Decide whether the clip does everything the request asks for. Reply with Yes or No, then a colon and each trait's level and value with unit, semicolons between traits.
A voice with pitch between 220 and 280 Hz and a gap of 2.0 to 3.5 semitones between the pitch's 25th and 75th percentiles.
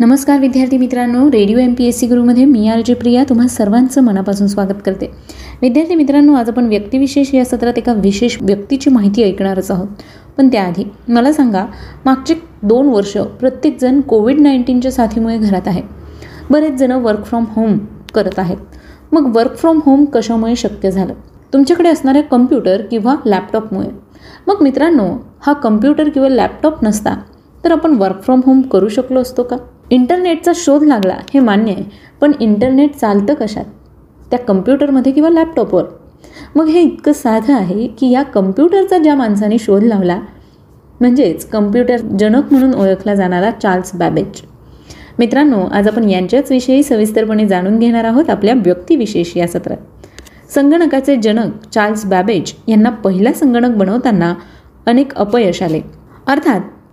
No: high, 245 Hz; average, 4.8 semitones